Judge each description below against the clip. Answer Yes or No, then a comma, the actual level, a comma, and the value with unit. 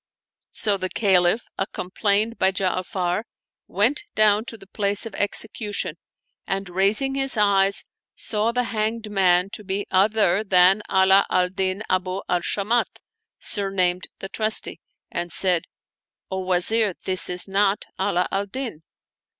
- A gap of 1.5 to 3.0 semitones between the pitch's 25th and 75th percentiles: Yes, narrow, 2.5 semitones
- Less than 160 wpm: Yes, average, 145 wpm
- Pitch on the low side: No, high, 195 Hz